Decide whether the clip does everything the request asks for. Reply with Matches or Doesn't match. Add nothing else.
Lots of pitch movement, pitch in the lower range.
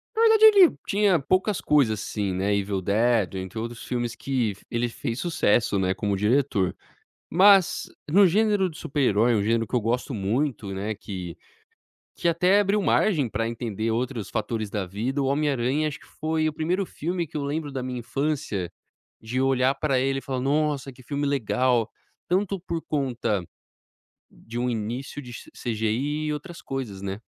Matches